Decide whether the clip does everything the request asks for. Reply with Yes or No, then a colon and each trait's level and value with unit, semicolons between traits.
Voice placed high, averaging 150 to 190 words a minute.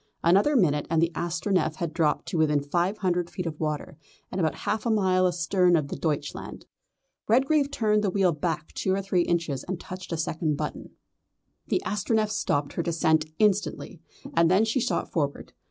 No: medium, 175 Hz; average, 185 wpm